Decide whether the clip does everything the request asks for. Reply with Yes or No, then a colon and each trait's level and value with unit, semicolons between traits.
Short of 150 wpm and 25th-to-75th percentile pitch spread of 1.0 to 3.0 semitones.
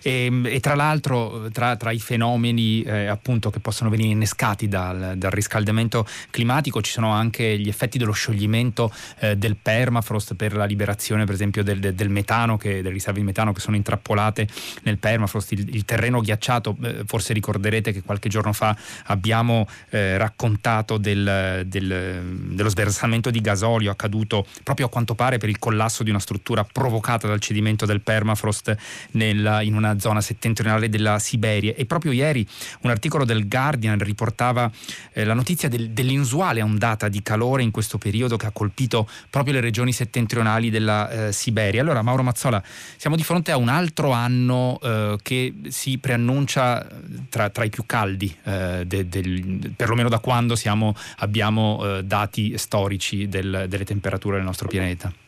No: average, 165 wpm; narrow, 2.4 semitones